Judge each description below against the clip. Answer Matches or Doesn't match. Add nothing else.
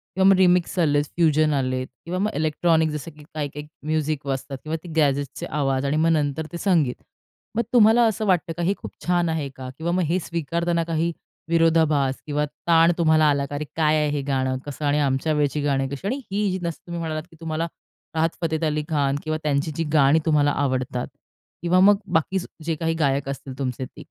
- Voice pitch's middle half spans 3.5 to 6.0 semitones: Doesn't match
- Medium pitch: Matches